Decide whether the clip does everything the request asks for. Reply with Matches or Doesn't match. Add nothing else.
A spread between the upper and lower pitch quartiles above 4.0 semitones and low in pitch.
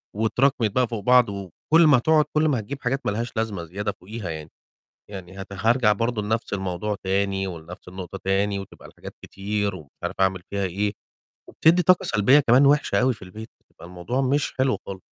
Matches